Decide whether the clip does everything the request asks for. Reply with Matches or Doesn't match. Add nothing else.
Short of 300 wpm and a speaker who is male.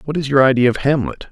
Matches